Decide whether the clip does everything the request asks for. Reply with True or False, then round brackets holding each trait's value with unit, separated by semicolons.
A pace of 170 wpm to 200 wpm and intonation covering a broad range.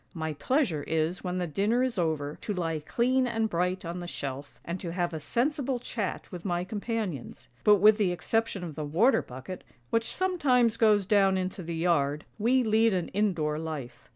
True (185 wpm; 5.7 semitones)